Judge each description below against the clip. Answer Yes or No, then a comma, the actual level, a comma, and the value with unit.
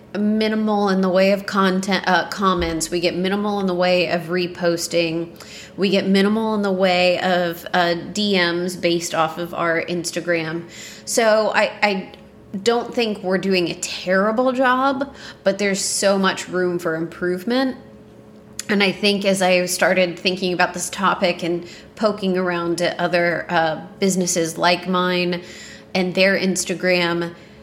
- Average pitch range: No, narrow, 2.2 semitones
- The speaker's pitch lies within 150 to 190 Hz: Yes, medium, 185 Hz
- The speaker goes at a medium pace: Yes, average, 150 wpm